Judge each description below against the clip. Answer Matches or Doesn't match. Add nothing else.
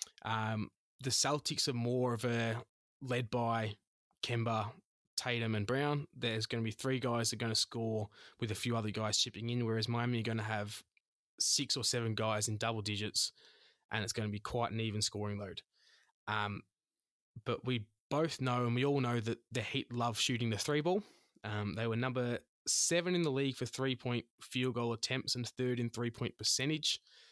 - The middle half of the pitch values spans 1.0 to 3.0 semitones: Matches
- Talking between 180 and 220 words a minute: Matches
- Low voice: Matches